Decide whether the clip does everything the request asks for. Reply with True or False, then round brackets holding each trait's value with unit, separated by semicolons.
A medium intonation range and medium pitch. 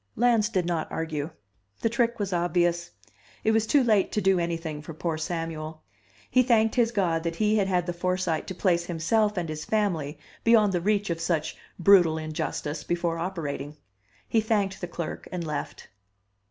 True (4.3 semitones; 175 Hz)